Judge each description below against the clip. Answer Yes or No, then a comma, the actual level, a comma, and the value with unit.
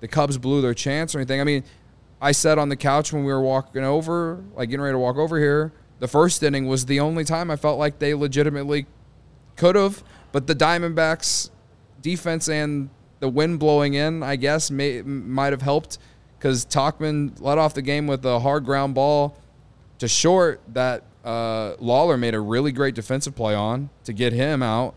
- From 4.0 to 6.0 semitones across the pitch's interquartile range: No, narrow, 2.5 semitones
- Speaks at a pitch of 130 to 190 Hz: Yes, medium, 140 Hz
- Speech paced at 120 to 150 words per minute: No, average, 195 wpm